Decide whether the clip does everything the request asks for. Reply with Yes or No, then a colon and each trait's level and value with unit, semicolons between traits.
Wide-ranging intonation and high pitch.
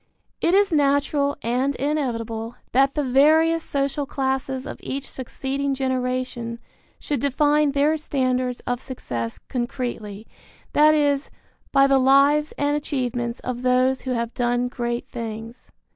No: average, 2.7 semitones; very high, 265 Hz